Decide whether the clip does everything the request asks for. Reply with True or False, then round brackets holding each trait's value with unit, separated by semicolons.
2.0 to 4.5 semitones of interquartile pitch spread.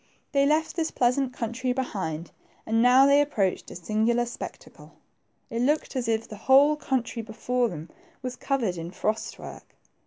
True (3.5 semitones)